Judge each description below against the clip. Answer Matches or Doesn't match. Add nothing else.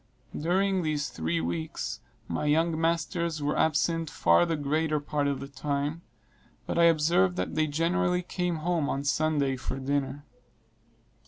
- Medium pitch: Matches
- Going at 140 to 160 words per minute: Matches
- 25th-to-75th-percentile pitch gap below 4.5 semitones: Matches